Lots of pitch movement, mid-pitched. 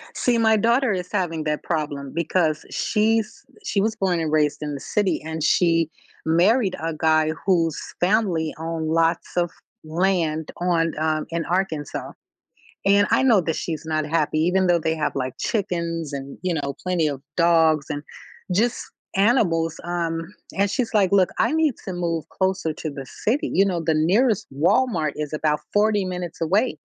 No: average, 3.8 semitones; medium, 170 Hz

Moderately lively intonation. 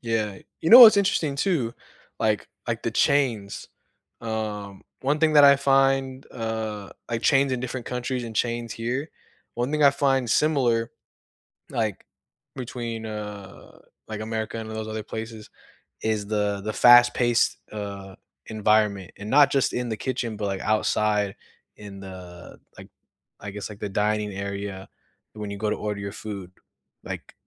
Yes: average, 3.5 semitones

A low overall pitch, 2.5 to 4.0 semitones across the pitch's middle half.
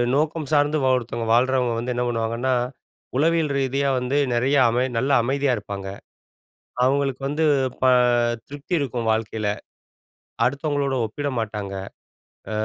Yes: low, 130 Hz; average, 3.4 semitones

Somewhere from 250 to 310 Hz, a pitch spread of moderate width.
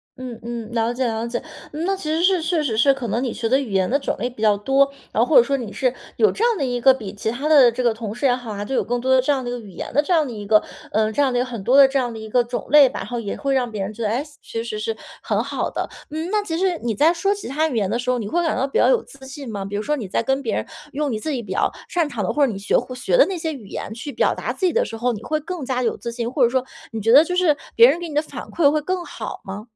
Yes: very high, 255 Hz; average, 4.8 semitones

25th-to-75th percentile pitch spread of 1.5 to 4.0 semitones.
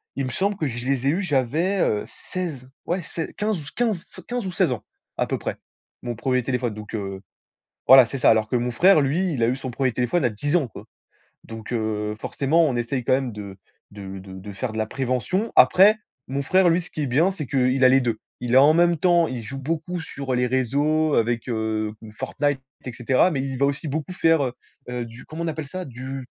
No: average, 5.3 semitones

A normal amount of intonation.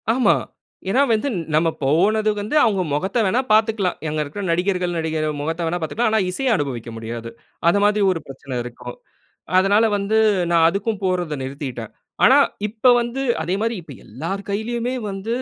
No: wide, 5.9 semitones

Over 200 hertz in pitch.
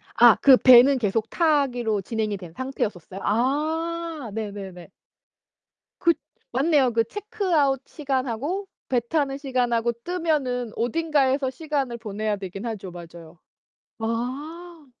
Yes: very high, 255 Hz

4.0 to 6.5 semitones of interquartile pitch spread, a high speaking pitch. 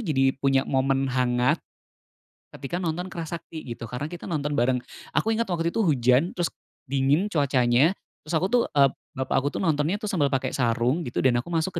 No: average, 4.5 semitones; medium, 145 Hz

